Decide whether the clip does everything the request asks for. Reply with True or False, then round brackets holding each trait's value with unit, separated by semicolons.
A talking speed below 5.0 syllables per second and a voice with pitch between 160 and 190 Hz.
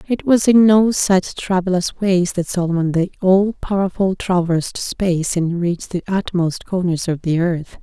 True (4.5 syllables/s; 185 Hz)